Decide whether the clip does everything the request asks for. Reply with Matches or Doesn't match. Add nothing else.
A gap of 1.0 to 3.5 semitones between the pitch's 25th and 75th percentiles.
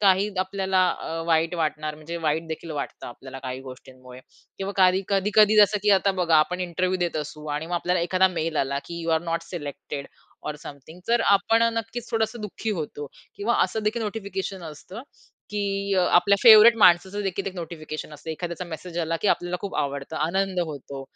Doesn't match